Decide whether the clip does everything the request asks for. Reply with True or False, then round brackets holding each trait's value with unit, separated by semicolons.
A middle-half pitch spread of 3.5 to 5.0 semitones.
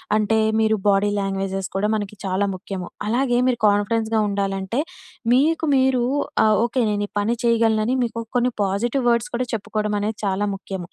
False (3.1 semitones)